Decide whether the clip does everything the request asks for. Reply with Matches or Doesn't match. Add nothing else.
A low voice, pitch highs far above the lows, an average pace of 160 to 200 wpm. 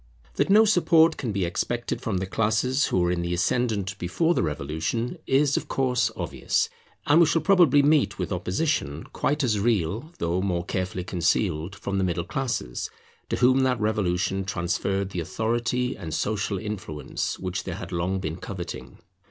Matches